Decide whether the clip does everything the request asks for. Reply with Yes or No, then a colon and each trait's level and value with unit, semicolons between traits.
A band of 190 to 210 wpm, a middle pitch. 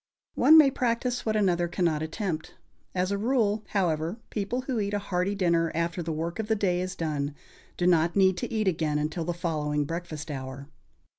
Yes: average, 195 wpm; medium, 175 Hz